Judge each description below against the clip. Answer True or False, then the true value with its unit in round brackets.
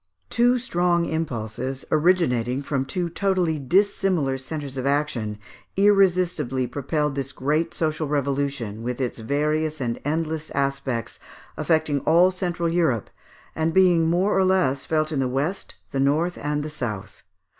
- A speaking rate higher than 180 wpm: False (140 wpm)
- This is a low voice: False (150 Hz)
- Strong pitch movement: False (4.2 semitones)